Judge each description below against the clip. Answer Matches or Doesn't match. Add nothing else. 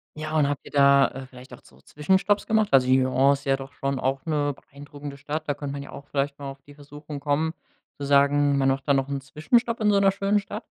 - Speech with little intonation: Matches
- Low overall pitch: Doesn't match